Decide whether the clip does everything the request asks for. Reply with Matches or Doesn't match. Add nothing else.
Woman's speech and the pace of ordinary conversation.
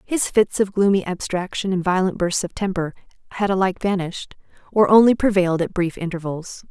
Matches